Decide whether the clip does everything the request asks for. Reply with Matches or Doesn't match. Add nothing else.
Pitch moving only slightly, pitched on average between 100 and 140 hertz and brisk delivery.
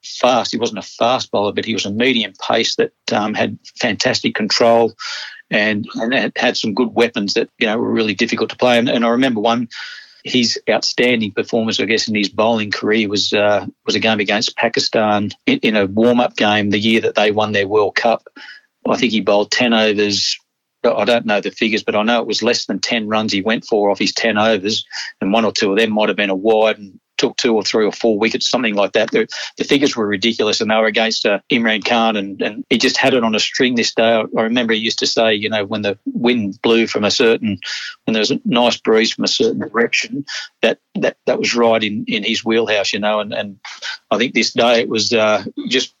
Matches